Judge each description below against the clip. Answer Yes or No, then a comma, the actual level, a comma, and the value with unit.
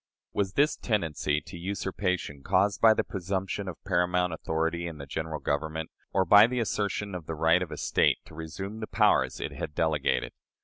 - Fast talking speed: No, average, 185 wpm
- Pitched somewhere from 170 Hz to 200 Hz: No, very low, 90 Hz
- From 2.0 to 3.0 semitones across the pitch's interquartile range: No, average, 3.7 semitones